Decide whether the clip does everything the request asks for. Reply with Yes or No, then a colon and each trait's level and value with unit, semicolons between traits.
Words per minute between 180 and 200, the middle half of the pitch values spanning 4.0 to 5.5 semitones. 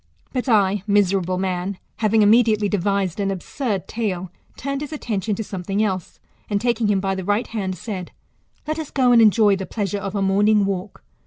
No: average, 185 wpm; narrow, 2.5 semitones